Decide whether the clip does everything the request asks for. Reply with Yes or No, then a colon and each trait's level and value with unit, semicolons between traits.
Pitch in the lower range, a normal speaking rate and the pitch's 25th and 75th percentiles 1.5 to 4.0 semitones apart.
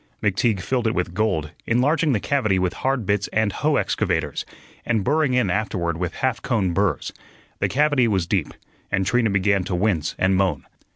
No: low, 105 Hz; average, 180 wpm; average, 4.9 semitones